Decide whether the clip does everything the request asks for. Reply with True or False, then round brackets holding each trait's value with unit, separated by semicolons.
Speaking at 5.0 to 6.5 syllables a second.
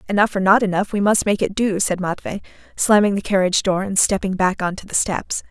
True (5.9 syllables/s)